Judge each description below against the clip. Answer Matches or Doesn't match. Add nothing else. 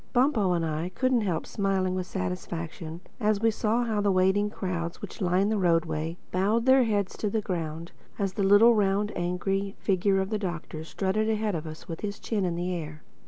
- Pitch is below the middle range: Doesn't match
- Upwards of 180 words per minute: Matches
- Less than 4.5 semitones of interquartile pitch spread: Matches